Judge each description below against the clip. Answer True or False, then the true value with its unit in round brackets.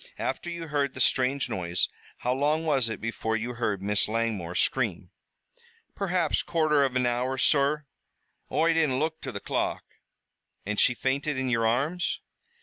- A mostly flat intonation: False (4.8 semitones)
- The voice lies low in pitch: True (130 Hz)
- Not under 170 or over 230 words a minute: False (160 wpm)